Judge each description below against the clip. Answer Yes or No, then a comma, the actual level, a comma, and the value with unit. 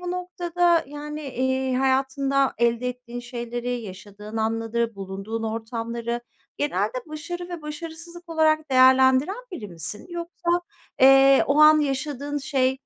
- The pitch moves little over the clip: No, average, 4.6 semitones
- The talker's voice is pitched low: No, very high, 265 Hz